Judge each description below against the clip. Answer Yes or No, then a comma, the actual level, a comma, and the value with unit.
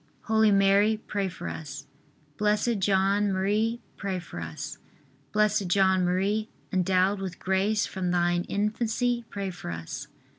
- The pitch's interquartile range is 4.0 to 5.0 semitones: No, narrow, 2.5 semitones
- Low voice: No, high, 195 Hz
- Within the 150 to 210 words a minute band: No, slow, 135 wpm